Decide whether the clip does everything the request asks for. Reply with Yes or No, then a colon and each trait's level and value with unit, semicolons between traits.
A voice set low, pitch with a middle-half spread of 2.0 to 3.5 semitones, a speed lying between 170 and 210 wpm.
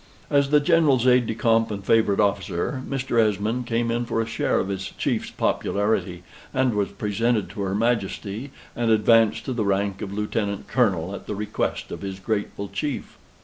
Yes: low, 110 Hz; average, 3.1 semitones; average, 185 wpm